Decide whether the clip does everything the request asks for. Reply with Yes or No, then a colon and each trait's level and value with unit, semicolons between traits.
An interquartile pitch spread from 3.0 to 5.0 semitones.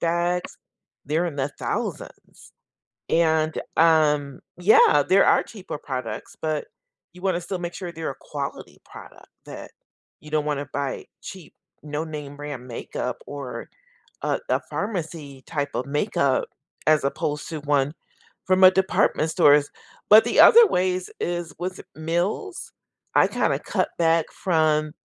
Yes: average, 3.4 semitones